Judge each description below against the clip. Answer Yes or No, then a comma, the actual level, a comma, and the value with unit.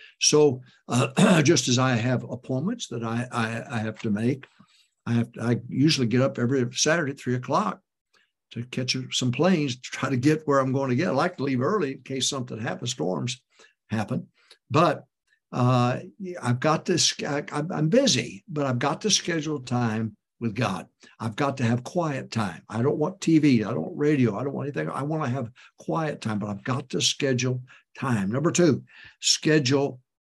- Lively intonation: No, average, 3.8 semitones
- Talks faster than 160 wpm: Yes, average, 195 wpm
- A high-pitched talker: No, low, 130 Hz